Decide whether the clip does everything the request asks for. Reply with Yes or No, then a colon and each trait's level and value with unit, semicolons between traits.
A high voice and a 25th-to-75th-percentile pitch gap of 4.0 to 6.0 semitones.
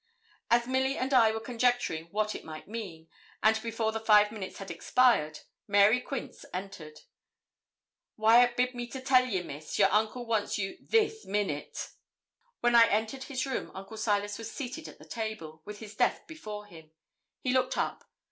No: high, 220 Hz; average, 3.6 semitones